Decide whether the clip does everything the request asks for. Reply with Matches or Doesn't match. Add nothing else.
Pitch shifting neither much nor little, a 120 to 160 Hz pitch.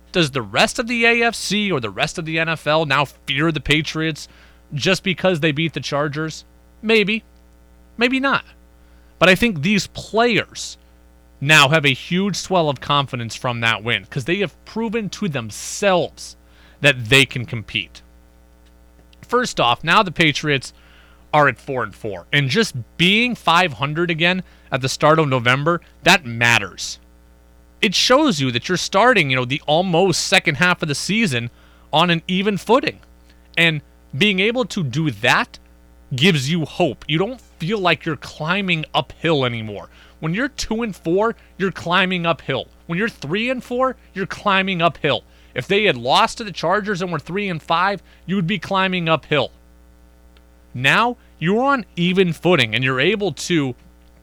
Doesn't match